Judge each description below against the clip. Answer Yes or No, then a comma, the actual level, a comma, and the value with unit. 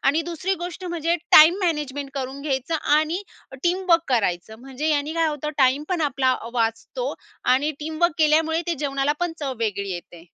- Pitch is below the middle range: No, very high, 300 Hz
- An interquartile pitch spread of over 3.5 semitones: Yes, average, 4.0 semitones